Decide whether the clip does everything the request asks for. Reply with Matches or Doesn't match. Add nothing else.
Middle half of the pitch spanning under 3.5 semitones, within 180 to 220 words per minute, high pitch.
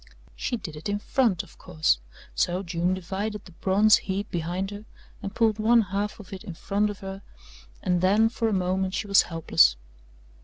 Matches